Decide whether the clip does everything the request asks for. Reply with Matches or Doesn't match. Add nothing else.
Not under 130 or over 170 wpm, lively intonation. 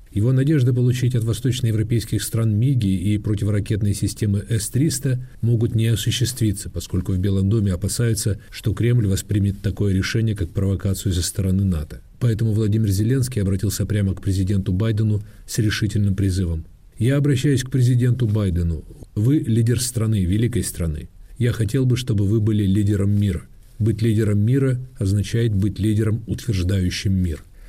Doesn't match